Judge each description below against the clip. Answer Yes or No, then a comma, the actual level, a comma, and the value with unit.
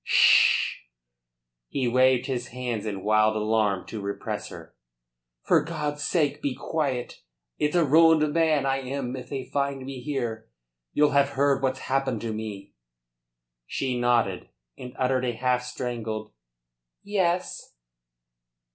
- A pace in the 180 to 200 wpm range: No, slow, 135 wpm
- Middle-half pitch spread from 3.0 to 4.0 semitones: Yes, average, 3.7 semitones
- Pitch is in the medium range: No, low, 130 Hz